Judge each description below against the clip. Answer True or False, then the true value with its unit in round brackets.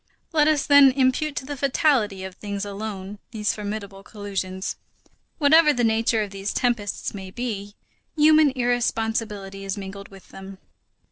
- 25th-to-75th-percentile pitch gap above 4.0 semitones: True (4.7 semitones)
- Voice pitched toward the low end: False (215 Hz)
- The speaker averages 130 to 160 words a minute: True (145 wpm)